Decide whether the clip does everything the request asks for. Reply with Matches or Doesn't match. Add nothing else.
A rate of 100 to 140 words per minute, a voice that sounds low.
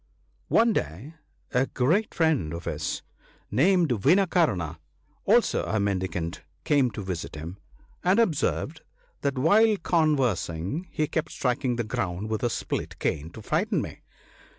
Matches